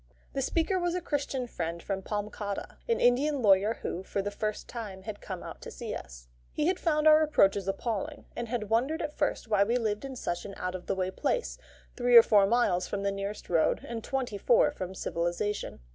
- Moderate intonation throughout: No, wide, 5.7 semitones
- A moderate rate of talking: No, fast, 215 wpm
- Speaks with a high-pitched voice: Yes, high, 215 Hz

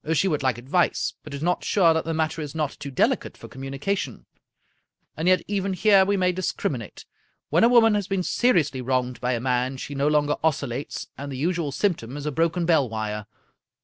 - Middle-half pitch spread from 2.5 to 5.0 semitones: No, wide, 5.5 semitones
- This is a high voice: No, medium, 150 Hz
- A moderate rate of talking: No, fast, 210 wpm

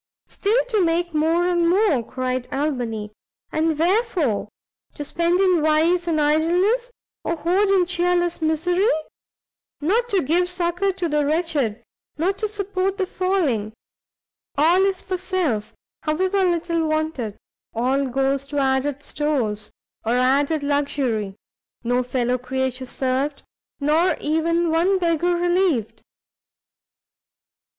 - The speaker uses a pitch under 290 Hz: No, very high, 320 Hz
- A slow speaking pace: Yes, slow, 125 wpm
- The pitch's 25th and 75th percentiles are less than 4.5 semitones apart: No, average, 4.9 semitones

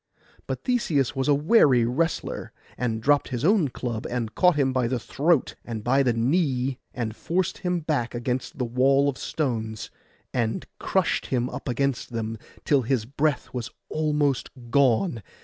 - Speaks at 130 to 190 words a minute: Yes, average, 165 wpm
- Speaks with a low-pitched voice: Yes, low, 130 Hz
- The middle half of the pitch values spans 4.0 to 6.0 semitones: No, average, 3.6 semitones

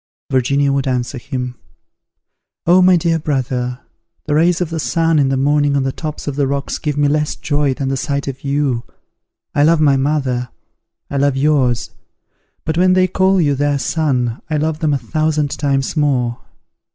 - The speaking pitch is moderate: Yes, medium, 145 Hz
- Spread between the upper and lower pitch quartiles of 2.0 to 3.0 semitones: Yes, narrow, 2.5 semitones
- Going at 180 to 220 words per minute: Yes, average, 185 wpm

